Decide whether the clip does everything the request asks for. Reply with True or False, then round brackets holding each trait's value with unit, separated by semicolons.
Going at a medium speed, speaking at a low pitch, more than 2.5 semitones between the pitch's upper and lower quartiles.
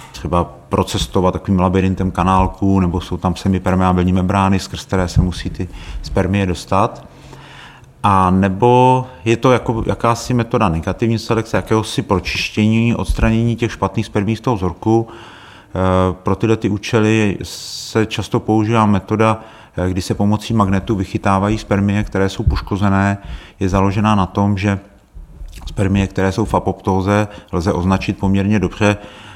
True (135 wpm; 100 Hz; 2.9 semitones)